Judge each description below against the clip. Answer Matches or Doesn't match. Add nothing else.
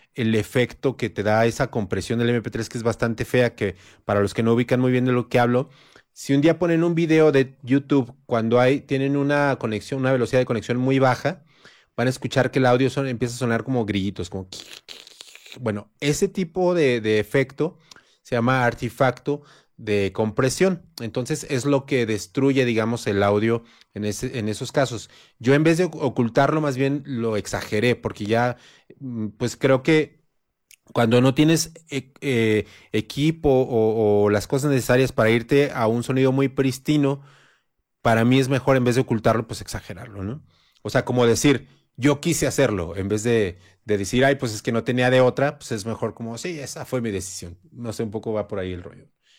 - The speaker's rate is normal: Doesn't match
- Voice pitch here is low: Matches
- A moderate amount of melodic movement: Matches